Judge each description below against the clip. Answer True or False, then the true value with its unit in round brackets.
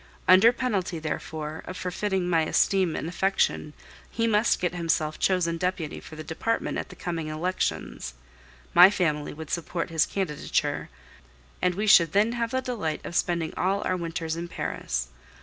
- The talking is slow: False (165 wpm)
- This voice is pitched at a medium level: True (175 Hz)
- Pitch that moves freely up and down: False (3.3 semitones)